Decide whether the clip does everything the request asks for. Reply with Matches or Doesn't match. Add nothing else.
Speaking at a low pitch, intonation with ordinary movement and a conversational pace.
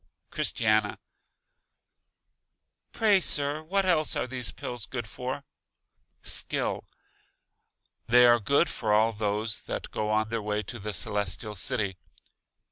Doesn't match